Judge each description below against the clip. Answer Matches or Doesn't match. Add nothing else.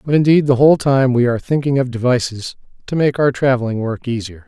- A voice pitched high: Doesn't match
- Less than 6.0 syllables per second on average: Doesn't match